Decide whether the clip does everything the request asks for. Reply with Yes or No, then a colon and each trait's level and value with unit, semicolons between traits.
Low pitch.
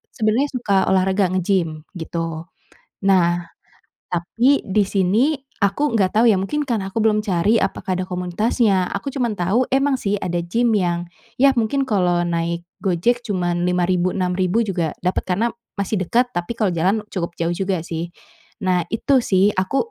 No: high, 190 Hz